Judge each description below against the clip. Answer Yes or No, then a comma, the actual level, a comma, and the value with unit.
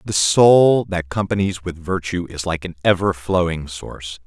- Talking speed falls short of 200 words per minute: Yes, average, 170 wpm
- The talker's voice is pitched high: No, very low, 90 Hz